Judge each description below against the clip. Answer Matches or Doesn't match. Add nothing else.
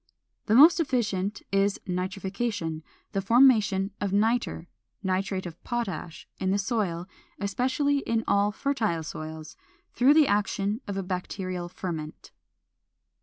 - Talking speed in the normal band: Doesn't match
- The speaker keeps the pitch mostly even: Doesn't match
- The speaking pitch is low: Doesn't match